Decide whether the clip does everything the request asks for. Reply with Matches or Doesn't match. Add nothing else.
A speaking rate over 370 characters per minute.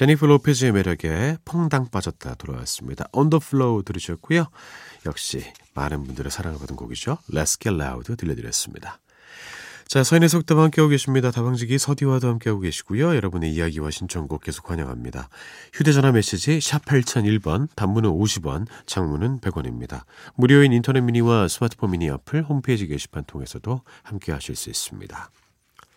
Matches